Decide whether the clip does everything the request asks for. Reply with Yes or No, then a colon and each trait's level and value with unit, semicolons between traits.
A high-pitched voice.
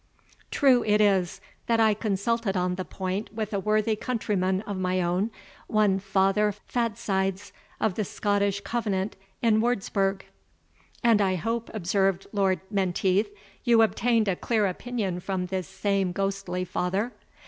Yes: high, 200 Hz